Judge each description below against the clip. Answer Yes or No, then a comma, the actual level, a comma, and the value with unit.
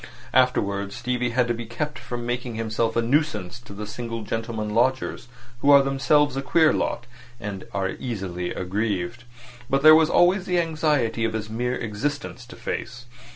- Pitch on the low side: Yes, low, 120 Hz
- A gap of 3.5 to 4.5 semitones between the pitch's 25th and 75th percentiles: Yes, average, 3.8 semitones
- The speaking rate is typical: Yes, average, 170 wpm